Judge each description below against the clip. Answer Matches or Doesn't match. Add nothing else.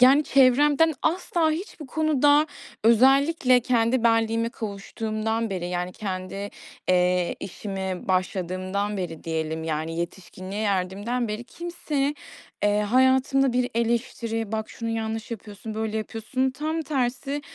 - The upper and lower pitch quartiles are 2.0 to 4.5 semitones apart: Doesn't match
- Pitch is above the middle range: Matches